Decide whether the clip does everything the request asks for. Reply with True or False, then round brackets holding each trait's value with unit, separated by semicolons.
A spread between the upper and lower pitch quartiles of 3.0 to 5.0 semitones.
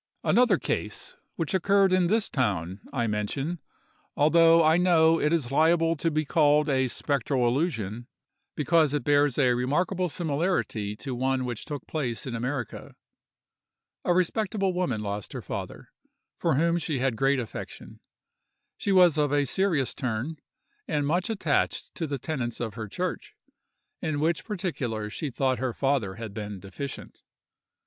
False (5.4 semitones)